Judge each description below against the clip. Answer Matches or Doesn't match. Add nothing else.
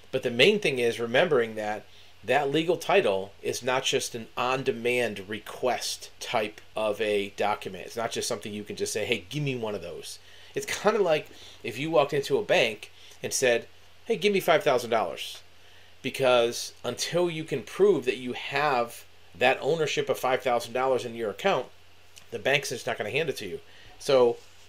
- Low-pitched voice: Matches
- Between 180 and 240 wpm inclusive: Matches